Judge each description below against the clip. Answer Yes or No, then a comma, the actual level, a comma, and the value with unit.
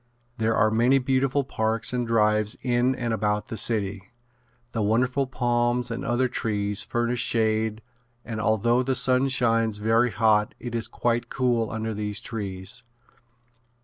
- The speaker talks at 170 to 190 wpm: No, average, 145 wpm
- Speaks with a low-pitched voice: Yes, low, 115 Hz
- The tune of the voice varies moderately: No, narrow, 2.2 semitones